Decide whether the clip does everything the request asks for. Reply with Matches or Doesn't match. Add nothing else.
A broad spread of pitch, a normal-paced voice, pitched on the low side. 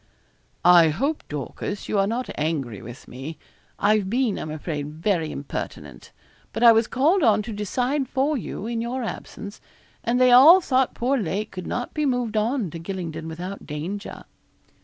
Doesn't match